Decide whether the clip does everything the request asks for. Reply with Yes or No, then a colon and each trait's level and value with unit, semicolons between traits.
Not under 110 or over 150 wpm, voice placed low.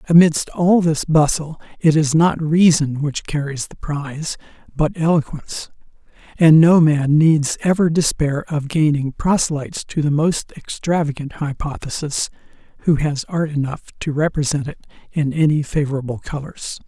No: average, 140 wpm; medium, 150 Hz